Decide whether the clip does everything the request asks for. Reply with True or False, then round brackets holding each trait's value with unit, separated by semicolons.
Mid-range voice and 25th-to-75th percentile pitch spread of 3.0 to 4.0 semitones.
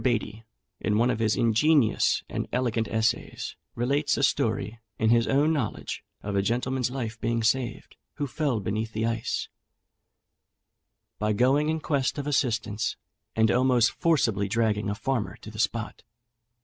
False (115 Hz; 3.3 semitones)